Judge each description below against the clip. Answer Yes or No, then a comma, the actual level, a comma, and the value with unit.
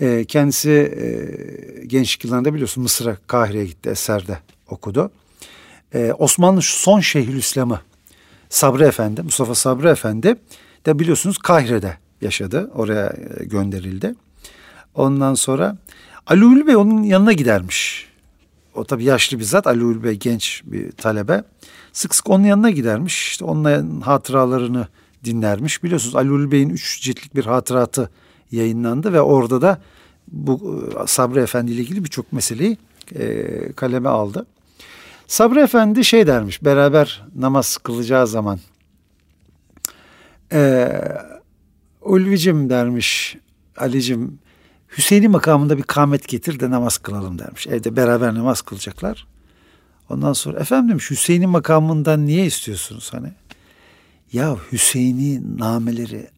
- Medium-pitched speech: No, low, 130 Hz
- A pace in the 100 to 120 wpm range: Yes, average, 115 wpm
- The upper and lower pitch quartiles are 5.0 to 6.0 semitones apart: Yes, wide, 5.6 semitones